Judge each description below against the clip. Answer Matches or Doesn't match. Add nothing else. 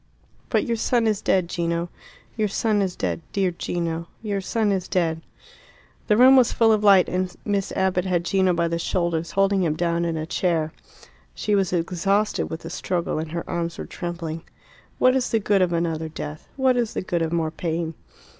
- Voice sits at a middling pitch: Matches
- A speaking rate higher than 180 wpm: Matches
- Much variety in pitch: Doesn't match